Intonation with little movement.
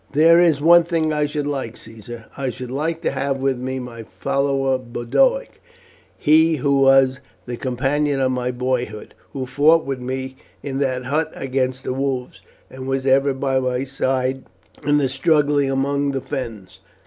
Yes: narrow, 2.0 semitones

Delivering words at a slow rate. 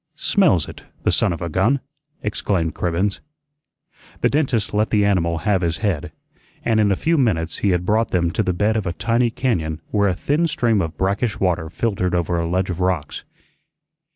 No: average, 195 wpm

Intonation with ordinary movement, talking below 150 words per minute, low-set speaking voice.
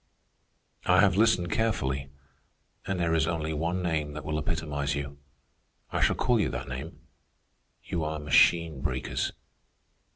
Yes: average, 3.3 semitones; average, 140 wpm; very low, 80 Hz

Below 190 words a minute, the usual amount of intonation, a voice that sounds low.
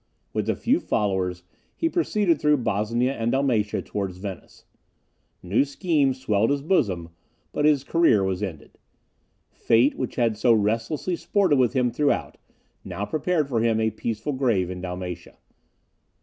No: average, 150 wpm; wide, 6.0 semitones; low, 115 Hz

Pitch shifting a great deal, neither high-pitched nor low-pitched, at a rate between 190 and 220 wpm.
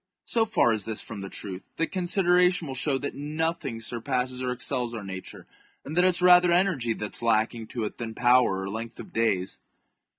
No: wide, 7.0 semitones; low, 125 Hz; fast, 205 wpm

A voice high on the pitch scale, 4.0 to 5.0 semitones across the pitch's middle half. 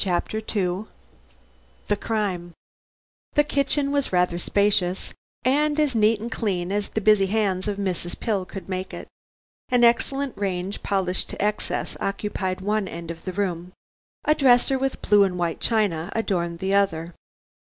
No: high, 200 Hz; average, 3.5 semitones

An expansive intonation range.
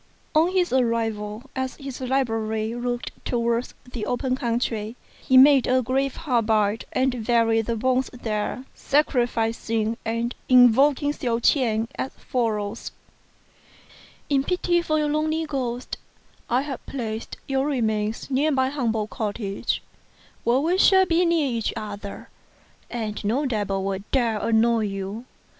No: average, 3.3 semitones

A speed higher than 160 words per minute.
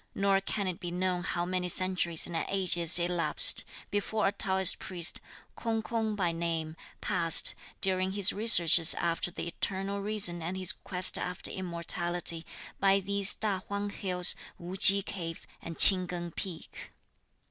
No: average, 150 wpm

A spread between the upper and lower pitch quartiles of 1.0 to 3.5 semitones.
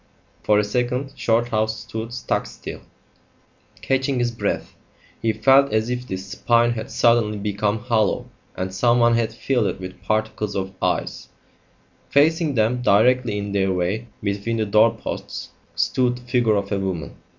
Yes: average, 3.2 semitones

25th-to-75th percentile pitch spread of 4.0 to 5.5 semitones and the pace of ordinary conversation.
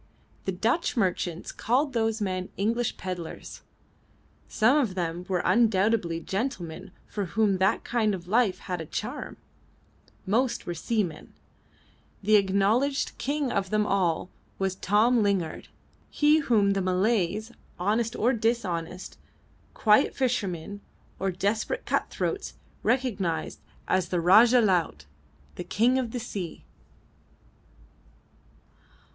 No: average, 4.3 semitones; slow, 120 wpm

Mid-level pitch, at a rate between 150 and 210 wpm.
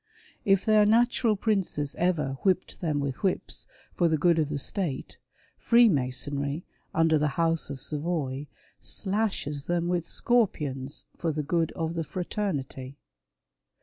No: medium, 165 Hz; average, 140 wpm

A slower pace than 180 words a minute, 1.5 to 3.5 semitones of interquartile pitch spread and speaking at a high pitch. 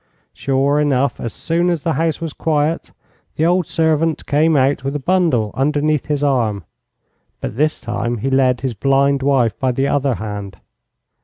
No: average, 170 wpm; average, 3.2 semitones; medium, 140 Hz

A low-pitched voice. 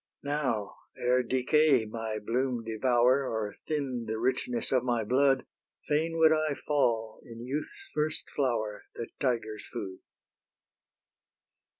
Yes: low, 125 Hz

